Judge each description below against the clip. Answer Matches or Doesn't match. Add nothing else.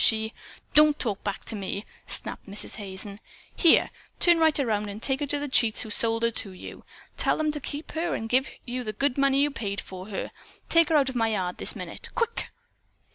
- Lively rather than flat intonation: Matches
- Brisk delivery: Matches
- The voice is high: Matches